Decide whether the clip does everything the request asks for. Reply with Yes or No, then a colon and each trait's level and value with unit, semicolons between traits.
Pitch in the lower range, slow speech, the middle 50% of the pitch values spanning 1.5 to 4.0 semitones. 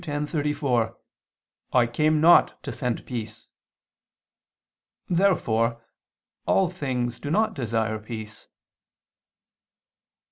No: low, 125 Hz; slow, 80 wpm; average, 5.0 semitones